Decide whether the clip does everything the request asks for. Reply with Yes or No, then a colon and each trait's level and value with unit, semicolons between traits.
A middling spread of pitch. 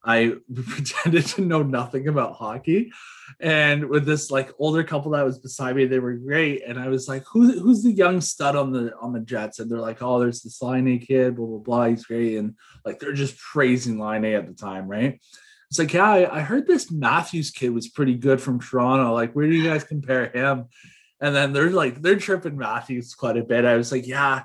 Yes: average, 3.9 semitones